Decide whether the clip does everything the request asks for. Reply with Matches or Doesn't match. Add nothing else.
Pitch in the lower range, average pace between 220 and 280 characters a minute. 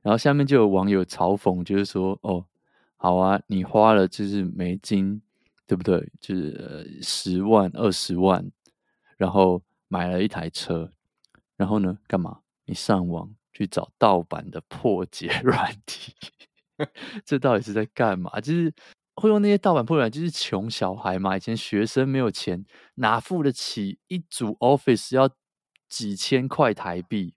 Matches